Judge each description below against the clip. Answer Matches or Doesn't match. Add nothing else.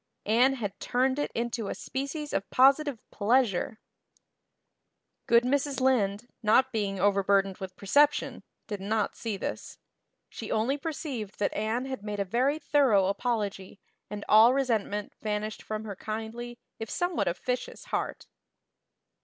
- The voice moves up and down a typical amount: Matches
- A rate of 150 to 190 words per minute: Doesn't match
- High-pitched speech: Matches